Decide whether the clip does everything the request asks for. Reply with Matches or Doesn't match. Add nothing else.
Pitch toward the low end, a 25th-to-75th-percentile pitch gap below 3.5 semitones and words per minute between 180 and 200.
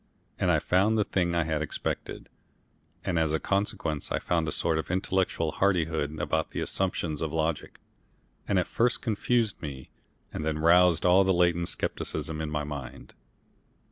Doesn't match